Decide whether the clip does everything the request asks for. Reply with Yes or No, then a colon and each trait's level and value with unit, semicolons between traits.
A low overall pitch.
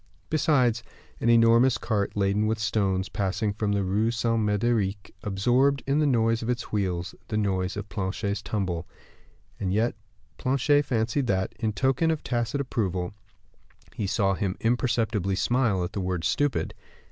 Yes: low, 110 Hz